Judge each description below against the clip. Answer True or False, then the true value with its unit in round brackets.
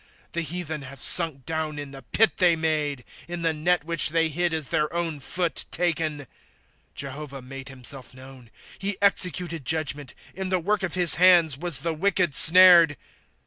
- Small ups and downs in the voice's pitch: False (3.7 semitones)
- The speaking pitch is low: False (160 Hz)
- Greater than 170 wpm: True (180 wpm)